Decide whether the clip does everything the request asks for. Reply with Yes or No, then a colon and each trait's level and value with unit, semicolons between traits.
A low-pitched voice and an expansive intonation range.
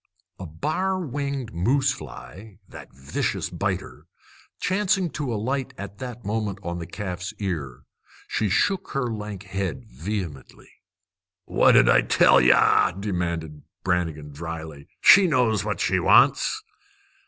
Yes: low, 100 Hz; wide, 7.5 semitones